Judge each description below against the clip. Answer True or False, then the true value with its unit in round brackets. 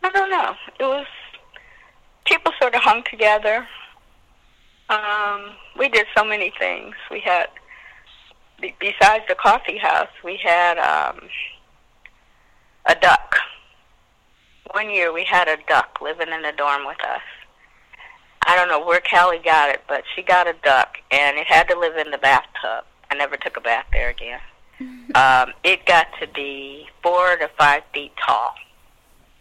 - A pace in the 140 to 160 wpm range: True (155 wpm)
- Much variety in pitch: True (6.0 semitones)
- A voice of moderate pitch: True (175 Hz)